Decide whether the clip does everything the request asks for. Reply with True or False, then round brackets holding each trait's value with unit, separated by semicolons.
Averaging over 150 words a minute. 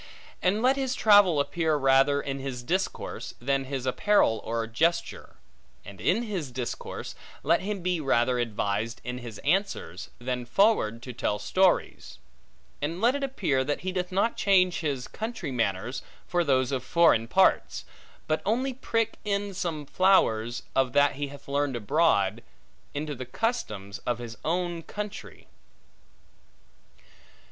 False (145 wpm)